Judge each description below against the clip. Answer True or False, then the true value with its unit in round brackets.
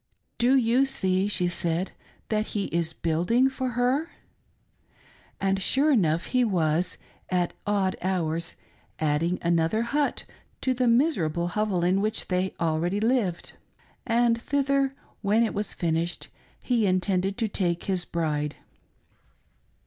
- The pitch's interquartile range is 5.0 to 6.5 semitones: True (5.5 semitones)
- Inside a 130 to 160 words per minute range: True (140 wpm)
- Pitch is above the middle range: True (195 Hz)